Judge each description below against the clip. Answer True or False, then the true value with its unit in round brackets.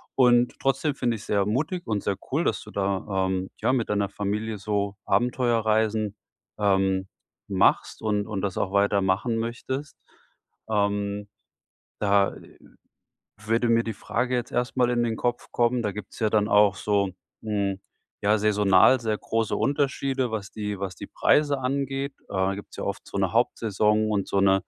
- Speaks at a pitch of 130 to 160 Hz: False (105 Hz)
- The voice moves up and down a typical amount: True (3.2 semitones)